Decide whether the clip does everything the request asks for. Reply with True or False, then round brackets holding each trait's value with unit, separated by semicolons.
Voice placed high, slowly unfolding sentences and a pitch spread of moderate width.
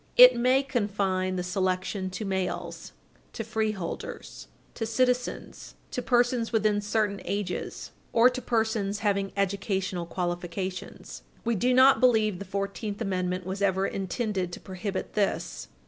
True (200 Hz; 130 wpm; 3.2 semitones)